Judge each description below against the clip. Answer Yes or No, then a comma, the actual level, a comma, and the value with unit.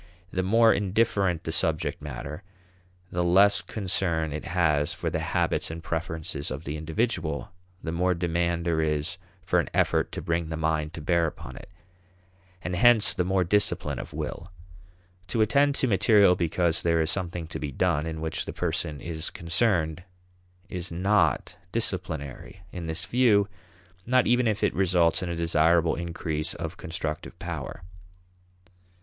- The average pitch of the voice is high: No, very low, 85 Hz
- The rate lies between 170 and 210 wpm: No, average, 160 wpm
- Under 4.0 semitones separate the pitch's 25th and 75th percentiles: Yes, average, 3.2 semitones